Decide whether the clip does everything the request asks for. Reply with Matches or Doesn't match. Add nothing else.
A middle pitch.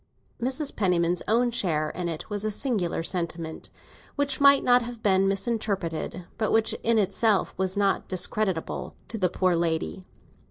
Doesn't match